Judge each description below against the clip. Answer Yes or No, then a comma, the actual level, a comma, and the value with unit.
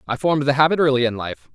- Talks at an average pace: No, fast, 270 wpm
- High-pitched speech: No, medium, 140 Hz